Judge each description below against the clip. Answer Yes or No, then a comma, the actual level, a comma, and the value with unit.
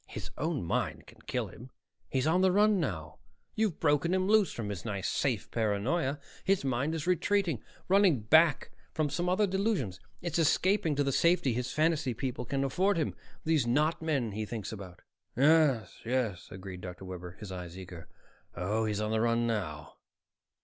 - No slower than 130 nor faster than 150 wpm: No, average, 175 wpm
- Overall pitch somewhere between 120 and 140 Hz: Yes, low, 135 Hz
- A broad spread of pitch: Yes, wide, 7.7 semitones